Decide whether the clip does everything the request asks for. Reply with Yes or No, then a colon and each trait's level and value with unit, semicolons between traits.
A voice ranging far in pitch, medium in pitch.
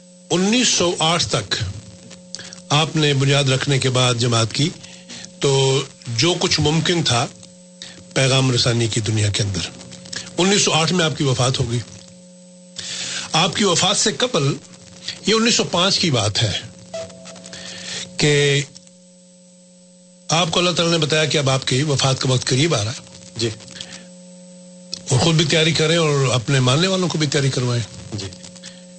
Yes: wide, 6.3 semitones; medium, 150 Hz